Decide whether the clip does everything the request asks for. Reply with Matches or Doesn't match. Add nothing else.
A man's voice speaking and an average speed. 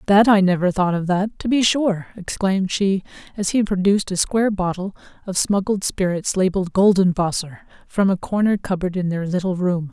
Doesn't match